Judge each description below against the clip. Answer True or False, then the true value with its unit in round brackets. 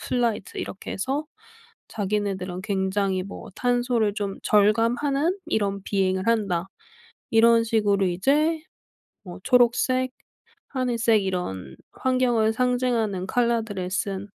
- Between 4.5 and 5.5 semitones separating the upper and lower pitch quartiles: False (4.1 semitones)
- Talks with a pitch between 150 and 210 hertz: False (220 Hz)